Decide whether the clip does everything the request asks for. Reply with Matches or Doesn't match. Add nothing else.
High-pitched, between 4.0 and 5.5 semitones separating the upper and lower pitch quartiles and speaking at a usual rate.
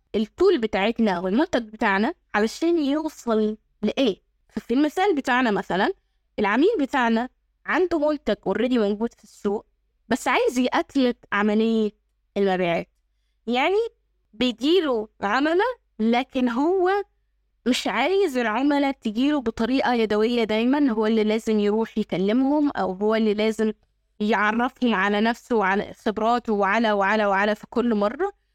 Matches